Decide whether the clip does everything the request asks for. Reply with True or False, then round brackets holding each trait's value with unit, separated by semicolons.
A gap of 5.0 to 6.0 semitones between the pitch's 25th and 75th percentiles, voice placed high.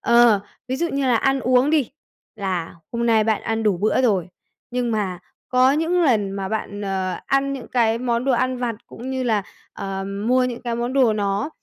False (3.8 semitones; 235 Hz)